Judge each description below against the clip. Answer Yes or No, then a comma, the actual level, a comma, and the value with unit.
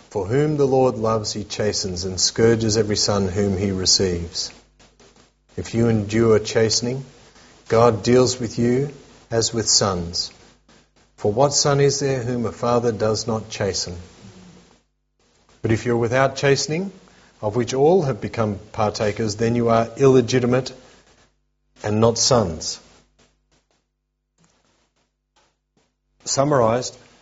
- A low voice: Yes, low, 115 Hz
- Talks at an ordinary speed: No, slow, 125 wpm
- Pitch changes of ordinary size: Yes, average, 3.5 semitones